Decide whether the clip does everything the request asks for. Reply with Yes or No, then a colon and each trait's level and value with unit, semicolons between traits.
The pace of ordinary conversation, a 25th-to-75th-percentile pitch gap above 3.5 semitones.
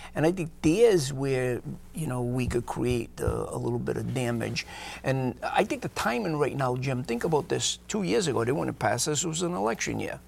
No: fast, 235 wpm; average, 4.3 semitones